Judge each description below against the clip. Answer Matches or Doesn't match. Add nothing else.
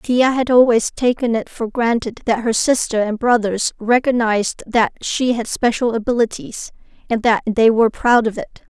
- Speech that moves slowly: Doesn't match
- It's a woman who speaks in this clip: Matches